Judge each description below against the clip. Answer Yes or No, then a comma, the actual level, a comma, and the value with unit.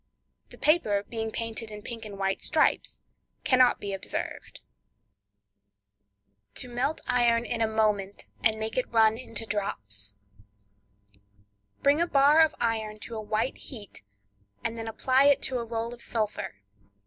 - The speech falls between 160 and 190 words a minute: No, average, 145 wpm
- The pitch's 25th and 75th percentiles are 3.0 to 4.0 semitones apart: Yes, average, 3.7 semitones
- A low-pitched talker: No, high, 220 Hz